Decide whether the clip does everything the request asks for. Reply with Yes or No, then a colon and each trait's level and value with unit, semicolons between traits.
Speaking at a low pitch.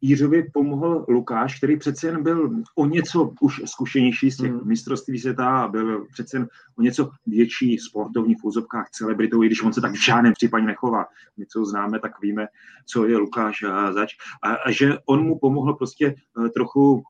Yes: low, 125 Hz